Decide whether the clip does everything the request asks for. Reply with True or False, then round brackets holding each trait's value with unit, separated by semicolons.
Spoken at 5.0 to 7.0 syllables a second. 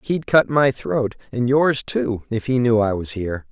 False (4.4 syllables/s)